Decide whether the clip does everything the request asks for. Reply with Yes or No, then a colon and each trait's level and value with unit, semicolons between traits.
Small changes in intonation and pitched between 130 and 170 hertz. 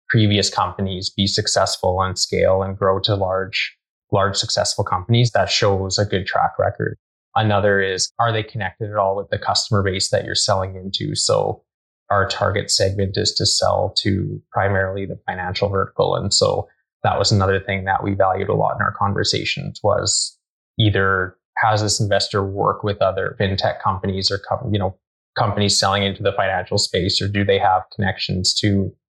No: narrow, 1.5 semitones; low, 100 Hz